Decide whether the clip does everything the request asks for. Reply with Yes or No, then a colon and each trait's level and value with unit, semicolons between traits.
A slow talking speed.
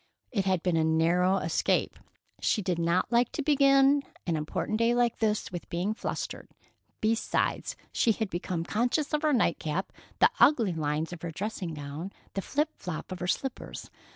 No: average, 180 wpm